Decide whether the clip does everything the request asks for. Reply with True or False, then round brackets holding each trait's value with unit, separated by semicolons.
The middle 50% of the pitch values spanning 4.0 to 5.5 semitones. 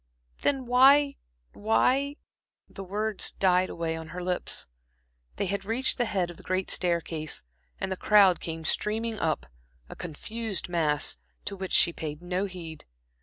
True (4.3 semitones)